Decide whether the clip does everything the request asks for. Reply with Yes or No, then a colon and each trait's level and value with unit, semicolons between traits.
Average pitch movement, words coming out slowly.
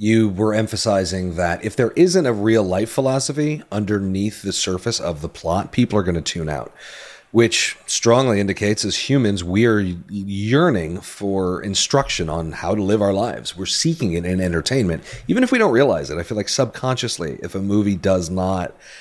No: average, 3.9 semitones; average, 185 wpm